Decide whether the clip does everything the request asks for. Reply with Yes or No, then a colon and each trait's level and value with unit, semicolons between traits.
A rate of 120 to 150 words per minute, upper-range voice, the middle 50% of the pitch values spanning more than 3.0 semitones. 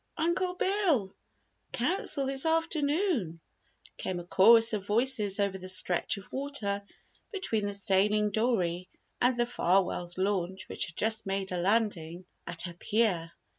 Yes: average, 140 wpm; high, 205 Hz; wide, 5.6 semitones